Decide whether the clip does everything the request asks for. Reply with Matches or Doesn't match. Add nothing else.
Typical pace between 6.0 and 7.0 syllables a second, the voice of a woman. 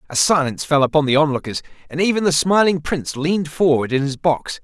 Doesn't match